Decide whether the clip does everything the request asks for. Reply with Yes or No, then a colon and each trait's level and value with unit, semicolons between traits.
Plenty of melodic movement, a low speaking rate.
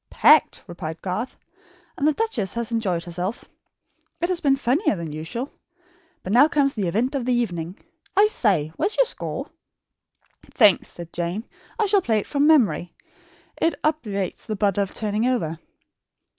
No: wide, 7.7 semitones; average, 165 wpm